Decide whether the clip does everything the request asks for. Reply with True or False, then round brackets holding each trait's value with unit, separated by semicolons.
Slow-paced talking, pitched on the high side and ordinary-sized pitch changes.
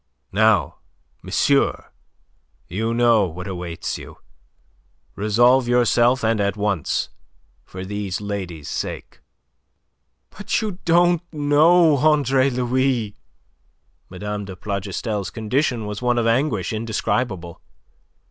False (100 wpm; 110 Hz; 4.5 semitones)